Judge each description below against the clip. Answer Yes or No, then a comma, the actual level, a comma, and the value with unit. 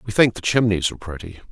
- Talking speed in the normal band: No, fast, 235 wpm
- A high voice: No, low, 100 Hz